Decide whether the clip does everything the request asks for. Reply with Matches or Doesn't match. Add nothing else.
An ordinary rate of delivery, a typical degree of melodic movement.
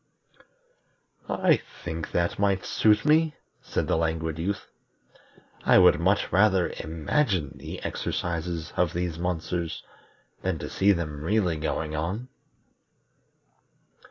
Doesn't match